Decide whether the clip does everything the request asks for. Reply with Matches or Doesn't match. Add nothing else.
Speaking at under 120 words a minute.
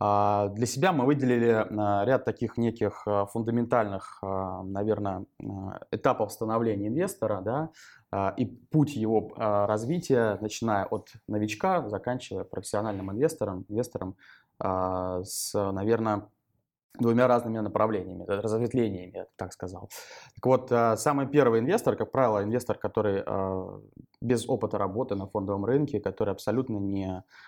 Matches